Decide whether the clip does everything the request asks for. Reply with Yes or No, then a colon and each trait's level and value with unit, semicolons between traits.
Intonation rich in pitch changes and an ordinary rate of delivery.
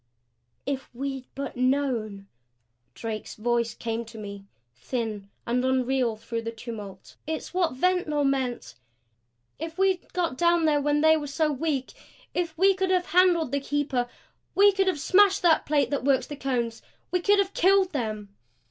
Yes: wide, 6.3 semitones; average, 165 wpm